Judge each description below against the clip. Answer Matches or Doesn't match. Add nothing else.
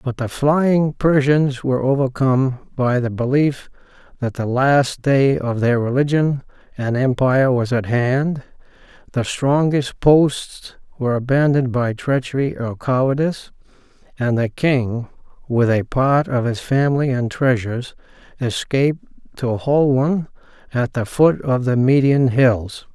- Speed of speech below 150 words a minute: Matches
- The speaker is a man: Matches